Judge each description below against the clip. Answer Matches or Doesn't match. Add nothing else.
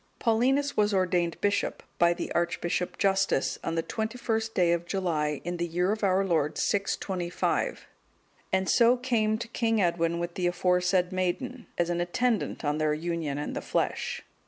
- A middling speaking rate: Matches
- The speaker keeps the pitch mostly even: Doesn't match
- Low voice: Doesn't match